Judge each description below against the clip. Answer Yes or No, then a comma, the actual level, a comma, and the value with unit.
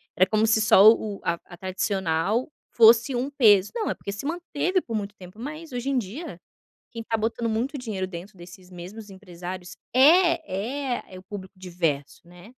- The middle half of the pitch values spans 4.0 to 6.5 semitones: Yes, average, 5.1 semitones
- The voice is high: Yes, high, 215 Hz